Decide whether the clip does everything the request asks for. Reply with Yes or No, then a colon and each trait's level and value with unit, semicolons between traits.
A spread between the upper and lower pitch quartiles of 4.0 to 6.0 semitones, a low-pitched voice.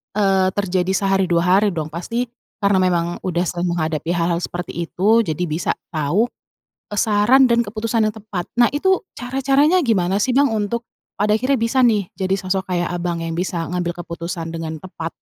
No: average, 4.3 semitones; high, 190 Hz